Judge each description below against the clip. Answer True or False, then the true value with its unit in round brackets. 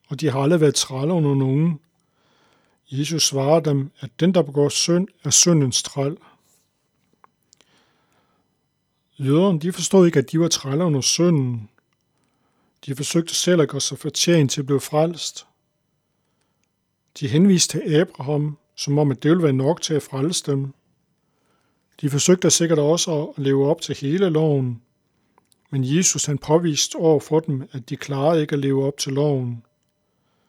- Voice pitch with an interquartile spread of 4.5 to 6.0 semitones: False (3.1 semitones)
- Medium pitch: True (150 Hz)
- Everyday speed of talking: True (160 wpm)